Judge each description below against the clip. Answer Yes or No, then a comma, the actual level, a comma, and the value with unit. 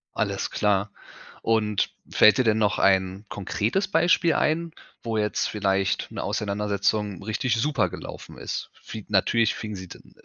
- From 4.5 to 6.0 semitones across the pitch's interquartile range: No, narrow, 2.4 semitones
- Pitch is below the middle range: Yes, low, 105 Hz